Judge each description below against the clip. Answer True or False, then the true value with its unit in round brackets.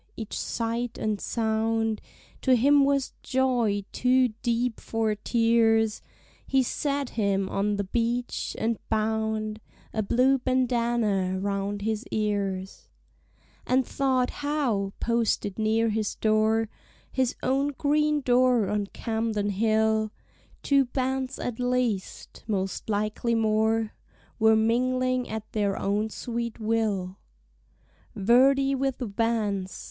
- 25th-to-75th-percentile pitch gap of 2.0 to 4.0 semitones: True (2.9 semitones)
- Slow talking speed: True (115 wpm)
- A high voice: True (225 Hz)